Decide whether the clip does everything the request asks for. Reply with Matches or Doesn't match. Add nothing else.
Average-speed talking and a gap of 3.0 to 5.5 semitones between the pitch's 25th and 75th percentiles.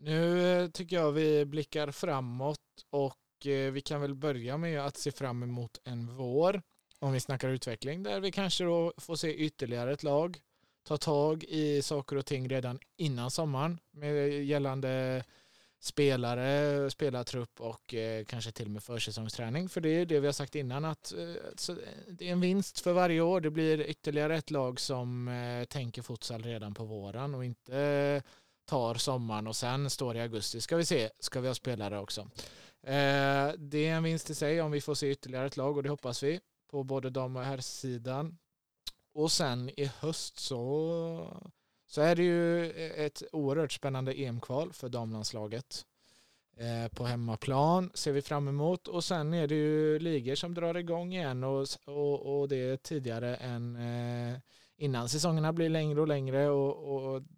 Matches